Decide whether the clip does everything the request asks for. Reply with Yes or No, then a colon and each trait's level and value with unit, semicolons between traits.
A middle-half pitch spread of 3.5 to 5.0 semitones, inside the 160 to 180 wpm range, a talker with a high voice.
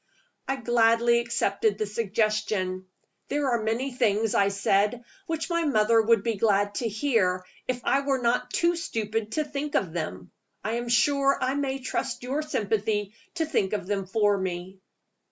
Yes: average, 4.4 semitones; average, 170 wpm; high, 225 Hz